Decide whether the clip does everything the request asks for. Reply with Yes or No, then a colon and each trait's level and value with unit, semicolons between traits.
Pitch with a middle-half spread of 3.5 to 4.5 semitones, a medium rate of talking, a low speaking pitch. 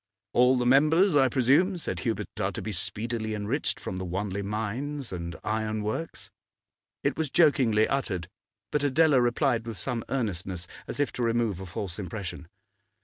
No: average, 5.3 semitones; average, 165 wpm; low, 115 Hz